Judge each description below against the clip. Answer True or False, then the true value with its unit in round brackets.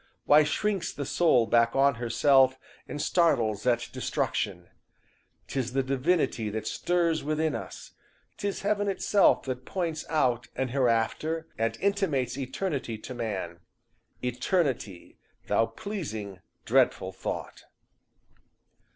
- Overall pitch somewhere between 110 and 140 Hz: True (135 Hz)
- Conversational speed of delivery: False (115 wpm)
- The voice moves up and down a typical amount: False (5.9 semitones)